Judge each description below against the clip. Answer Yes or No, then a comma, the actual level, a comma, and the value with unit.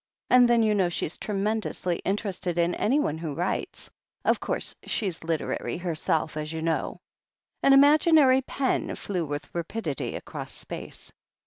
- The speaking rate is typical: Yes, average, 145 wpm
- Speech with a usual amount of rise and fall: No, wide, 5.9 semitones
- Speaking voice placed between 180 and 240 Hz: Yes, medium, 185 Hz